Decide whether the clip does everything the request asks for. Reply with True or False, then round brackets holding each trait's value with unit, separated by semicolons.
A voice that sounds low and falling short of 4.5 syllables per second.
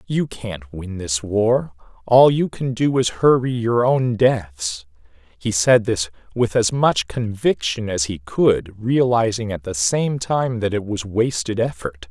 True (110 Hz; 3.7 syllables/s)